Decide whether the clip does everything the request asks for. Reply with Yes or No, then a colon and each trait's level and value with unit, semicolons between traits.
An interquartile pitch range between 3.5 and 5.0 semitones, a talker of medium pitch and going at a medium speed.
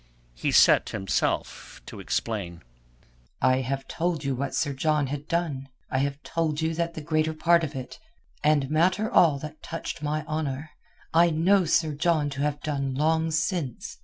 No: average, 2.9 semitones; medium, 150 Hz; average, 160 wpm